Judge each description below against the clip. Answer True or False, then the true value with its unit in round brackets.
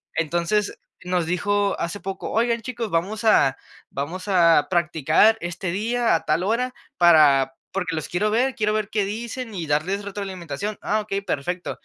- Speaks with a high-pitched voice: True (195 Hz)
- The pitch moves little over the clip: False (4.1 semitones)